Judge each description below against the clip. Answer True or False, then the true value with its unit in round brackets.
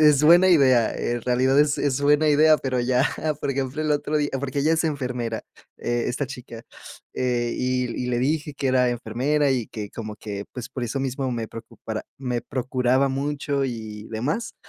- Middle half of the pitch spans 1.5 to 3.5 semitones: True (3.1 semitones)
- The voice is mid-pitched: False (130 Hz)